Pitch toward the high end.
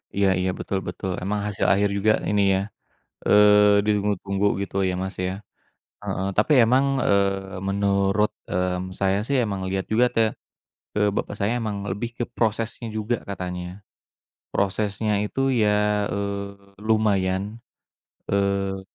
No: low, 100 Hz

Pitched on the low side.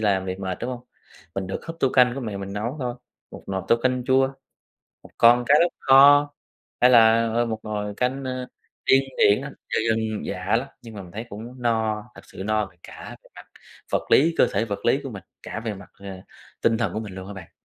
Yes: low, 115 Hz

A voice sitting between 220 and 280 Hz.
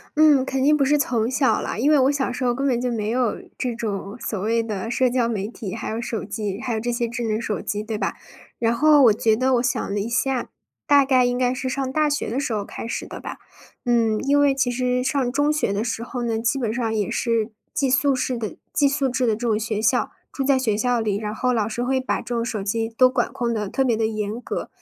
Yes: high, 240 Hz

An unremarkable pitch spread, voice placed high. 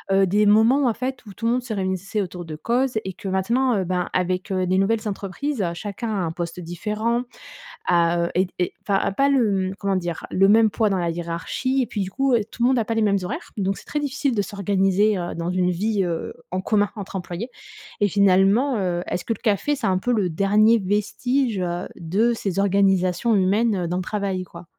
Yes: average, 3.7 semitones; high, 195 Hz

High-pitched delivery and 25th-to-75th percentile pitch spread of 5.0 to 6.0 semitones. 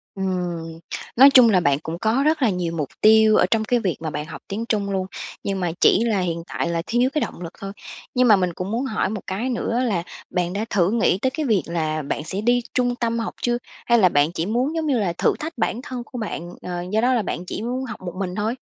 Yes: high, 210 Hz; wide, 5.4 semitones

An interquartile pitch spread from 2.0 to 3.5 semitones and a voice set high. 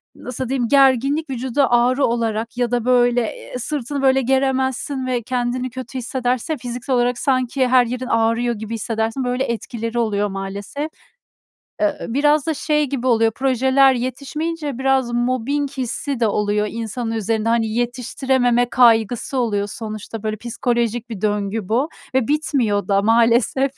Yes: average, 2.7 semitones; high, 245 Hz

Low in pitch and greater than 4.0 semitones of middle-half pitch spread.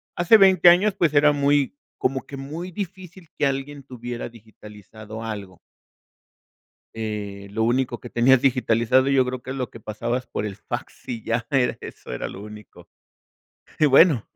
Yes: low, 125 Hz; average, 4.4 semitones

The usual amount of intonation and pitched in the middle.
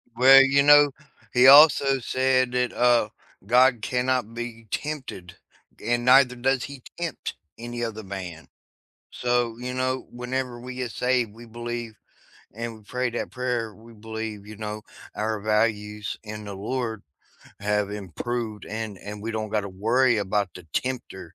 No: average, 3.1 semitones; low, 120 Hz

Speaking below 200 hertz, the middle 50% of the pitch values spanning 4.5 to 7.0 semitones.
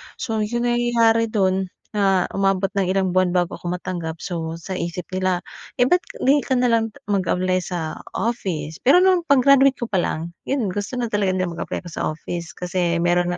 Yes: high, 190 Hz; average, 4.8 semitones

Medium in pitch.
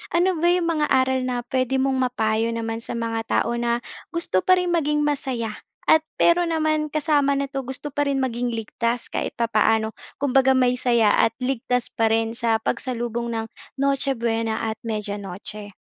No: very high, 250 Hz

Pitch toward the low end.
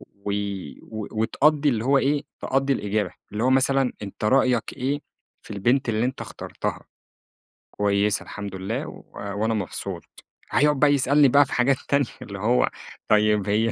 Yes: low, 120 Hz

